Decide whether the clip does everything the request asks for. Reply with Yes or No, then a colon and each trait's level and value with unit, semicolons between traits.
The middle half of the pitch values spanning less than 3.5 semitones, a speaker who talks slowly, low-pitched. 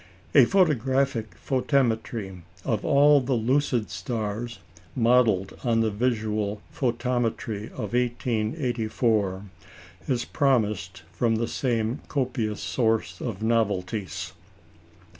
Yes: average, 2.9 semitones; slow, 95 wpm; low, 115 Hz